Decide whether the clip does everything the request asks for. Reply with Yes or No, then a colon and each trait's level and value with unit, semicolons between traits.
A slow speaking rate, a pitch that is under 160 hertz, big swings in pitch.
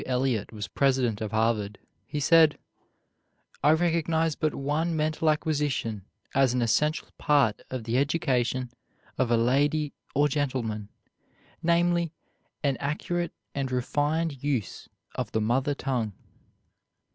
No: slow, 125 wpm; medium, 140 Hz; average, 4.5 semitones